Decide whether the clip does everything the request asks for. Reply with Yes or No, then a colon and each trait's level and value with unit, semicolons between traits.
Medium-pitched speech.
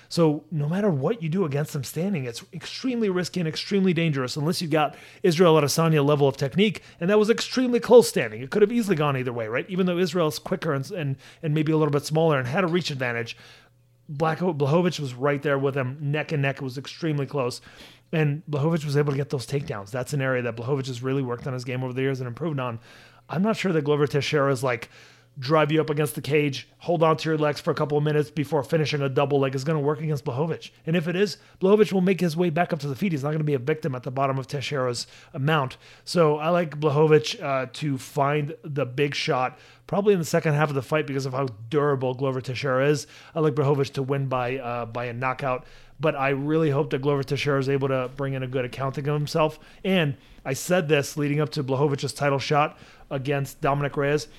Yes: medium, 145 Hz